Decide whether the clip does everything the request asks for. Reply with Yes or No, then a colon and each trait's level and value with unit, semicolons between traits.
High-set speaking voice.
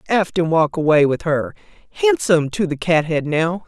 No: medium, 170 Hz